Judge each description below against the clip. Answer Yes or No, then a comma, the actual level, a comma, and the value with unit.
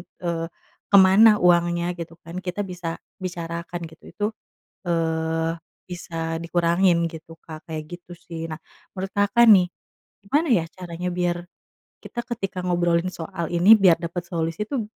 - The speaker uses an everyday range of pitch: No, narrow, 1.9 semitones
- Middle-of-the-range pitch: Yes, medium, 175 Hz